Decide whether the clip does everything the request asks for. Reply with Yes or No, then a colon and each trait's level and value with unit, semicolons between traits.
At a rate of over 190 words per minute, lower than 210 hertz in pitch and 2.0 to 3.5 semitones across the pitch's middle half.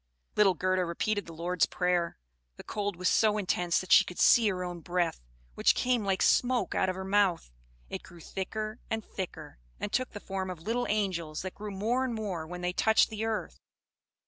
Yes: average, 200 wpm; high, 190 Hz; average, 3.2 semitones